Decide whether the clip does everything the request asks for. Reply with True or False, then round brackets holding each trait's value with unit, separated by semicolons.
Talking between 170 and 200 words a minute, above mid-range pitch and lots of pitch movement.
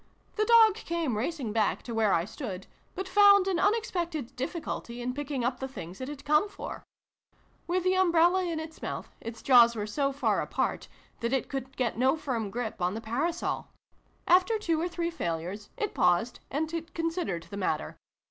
True (185 wpm; 280 Hz; 7.0 semitones)